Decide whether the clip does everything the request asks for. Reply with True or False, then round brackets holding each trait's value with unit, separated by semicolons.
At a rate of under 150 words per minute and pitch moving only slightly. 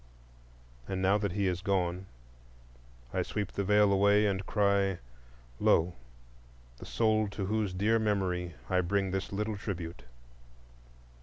True (135 wpm; 2.0 semitones)